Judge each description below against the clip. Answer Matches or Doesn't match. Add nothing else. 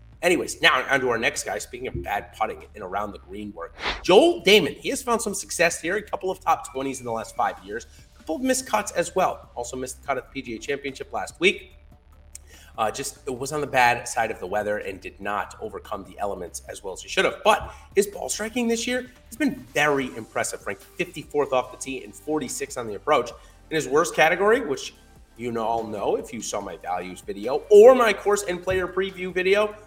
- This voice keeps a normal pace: Doesn't match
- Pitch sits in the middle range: Matches